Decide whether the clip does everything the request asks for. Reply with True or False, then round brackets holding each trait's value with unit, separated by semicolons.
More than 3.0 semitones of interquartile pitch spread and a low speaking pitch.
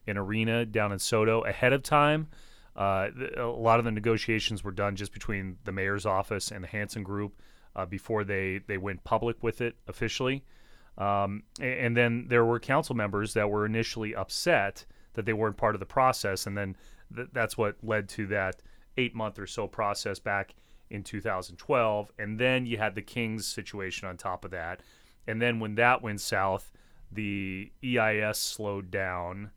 False (2.7 semitones; 105 Hz)